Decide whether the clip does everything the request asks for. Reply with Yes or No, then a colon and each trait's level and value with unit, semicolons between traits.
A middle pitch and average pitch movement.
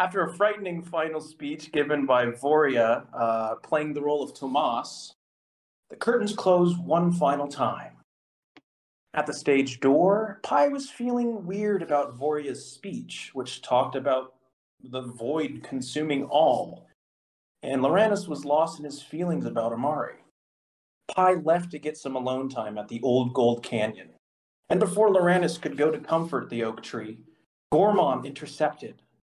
No: medium, 145 Hz; wide, 6.3 semitones